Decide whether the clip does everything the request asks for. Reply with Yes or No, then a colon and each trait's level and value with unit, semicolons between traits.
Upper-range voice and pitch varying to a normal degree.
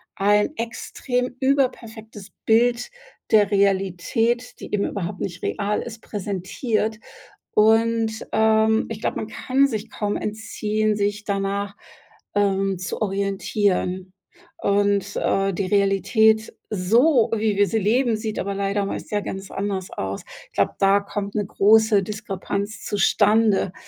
No: high, 210 Hz; narrow, 2.0 semitones